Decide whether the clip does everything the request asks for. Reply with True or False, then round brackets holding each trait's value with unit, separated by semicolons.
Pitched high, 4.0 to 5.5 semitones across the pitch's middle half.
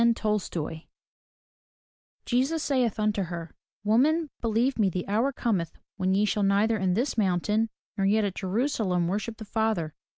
False (210 Hz; 3.5 semitones)